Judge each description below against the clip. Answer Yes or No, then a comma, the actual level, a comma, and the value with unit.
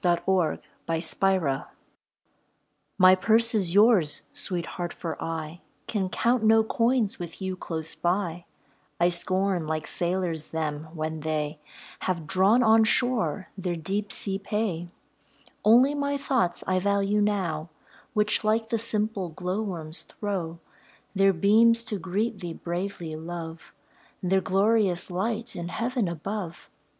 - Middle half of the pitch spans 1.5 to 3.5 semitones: No, average, 4.2 semitones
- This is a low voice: No, high, 190 Hz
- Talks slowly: Yes, slow, 130 wpm